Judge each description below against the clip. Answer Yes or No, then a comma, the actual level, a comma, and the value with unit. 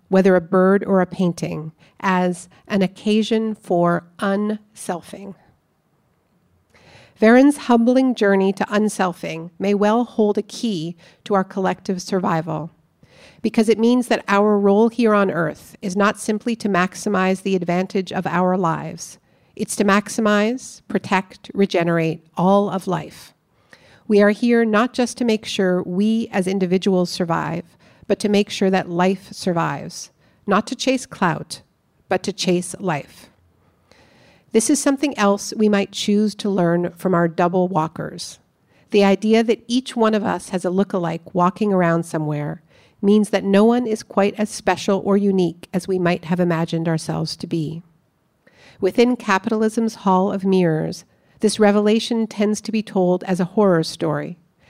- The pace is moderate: Yes, average, 150 wpm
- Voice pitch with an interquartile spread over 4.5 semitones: No, average, 3.0 semitones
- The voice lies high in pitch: Yes, high, 195 Hz